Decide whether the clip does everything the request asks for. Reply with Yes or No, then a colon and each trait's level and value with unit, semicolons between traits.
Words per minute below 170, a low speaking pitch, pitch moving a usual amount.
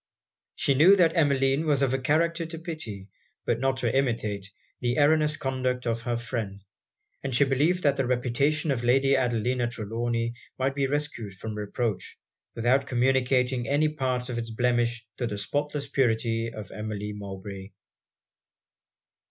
Yes: average, 150 wpm; low, 125 Hz; average, 3.3 semitones